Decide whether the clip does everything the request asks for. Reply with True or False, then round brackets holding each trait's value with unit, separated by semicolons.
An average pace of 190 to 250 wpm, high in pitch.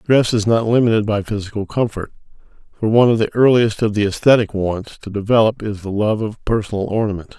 False (195 wpm; 110 Hz)